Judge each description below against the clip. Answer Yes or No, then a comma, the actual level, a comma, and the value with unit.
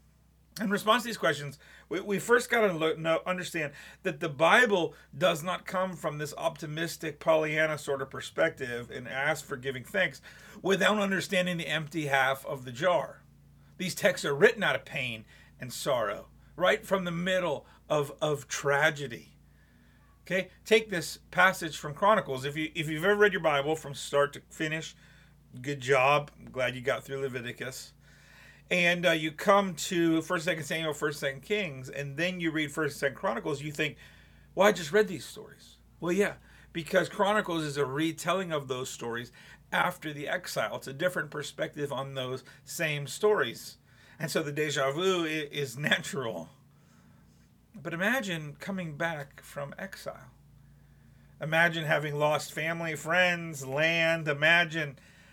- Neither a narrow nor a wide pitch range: Yes, average, 4.2 semitones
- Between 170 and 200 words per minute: No, average, 160 wpm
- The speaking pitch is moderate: Yes, medium, 155 Hz